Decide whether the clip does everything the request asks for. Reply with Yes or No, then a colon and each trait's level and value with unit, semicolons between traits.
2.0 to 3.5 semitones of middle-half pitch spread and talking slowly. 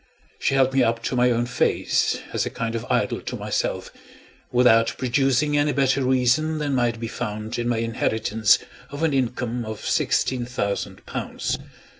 No: average, 2.7 semitones; average, 170 wpm